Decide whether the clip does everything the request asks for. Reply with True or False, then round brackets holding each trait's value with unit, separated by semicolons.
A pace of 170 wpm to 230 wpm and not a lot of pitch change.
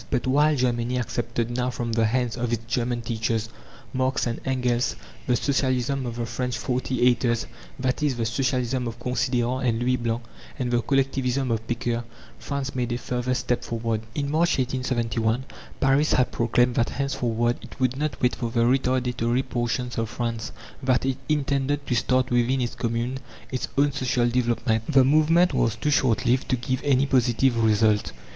True (175 wpm; 1.9 semitones)